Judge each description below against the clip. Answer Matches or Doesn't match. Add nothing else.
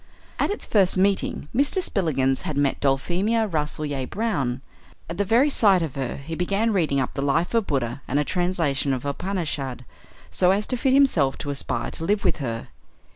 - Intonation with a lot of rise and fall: Matches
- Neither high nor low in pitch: Matches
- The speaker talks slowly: Doesn't match